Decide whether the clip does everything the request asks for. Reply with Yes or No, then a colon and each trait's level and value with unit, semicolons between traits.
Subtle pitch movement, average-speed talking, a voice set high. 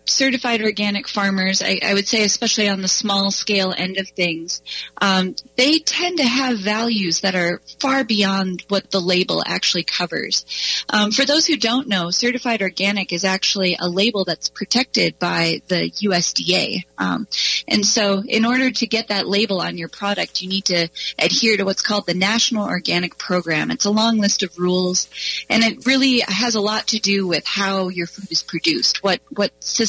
No: average, 3.6 semitones; average, 185 wpm; high, 200 Hz